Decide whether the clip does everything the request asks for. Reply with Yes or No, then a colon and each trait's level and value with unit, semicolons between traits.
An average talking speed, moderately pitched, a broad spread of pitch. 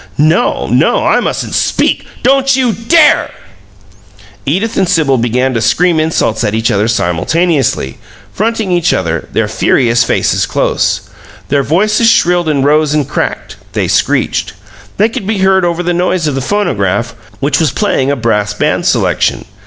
Yes: average, 160 wpm; medium, 155 Hz; wide, 7.6 semitones